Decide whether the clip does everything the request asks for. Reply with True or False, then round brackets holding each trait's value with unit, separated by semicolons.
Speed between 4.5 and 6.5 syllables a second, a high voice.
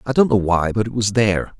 False (6.3 syllables/s; 110 Hz)